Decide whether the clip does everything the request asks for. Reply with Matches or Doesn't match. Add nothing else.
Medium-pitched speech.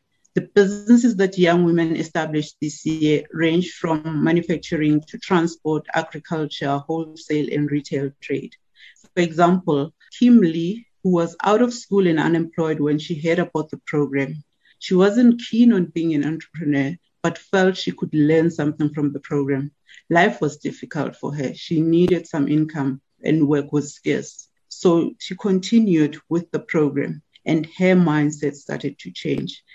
Matches